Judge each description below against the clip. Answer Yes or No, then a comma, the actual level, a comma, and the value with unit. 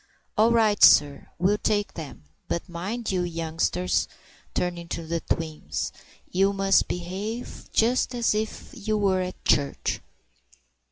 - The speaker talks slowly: Yes, slow, 115 wpm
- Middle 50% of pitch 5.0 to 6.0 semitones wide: No, average, 4.2 semitones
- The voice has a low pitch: No, medium, 185 Hz